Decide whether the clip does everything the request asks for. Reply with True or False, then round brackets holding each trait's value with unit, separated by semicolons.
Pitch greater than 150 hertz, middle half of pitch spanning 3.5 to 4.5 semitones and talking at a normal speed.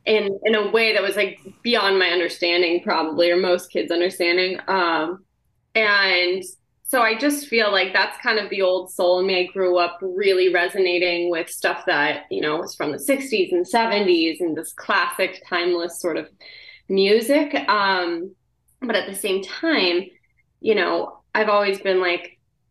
False (185 Hz; 2.8 semitones; 170 wpm)